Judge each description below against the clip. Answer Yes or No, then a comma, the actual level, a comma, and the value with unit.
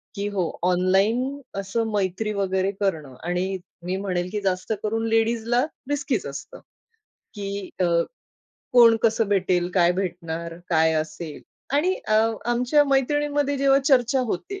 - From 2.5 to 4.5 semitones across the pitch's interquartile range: No, average, 5.1 semitones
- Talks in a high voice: Yes, high, 200 Hz